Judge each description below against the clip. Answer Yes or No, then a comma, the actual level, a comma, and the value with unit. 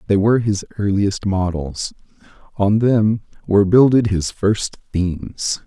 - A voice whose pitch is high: No, low, 100 Hz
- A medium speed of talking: No, slow, 125 wpm